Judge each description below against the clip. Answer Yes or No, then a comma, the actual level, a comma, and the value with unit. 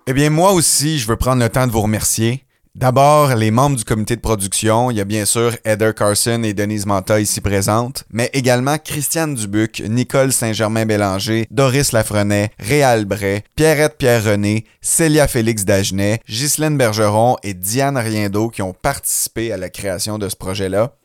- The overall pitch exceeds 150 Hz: No, low, 110 Hz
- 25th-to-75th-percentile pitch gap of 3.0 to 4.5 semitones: Yes, average, 4.0 semitones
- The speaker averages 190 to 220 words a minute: No, average, 170 wpm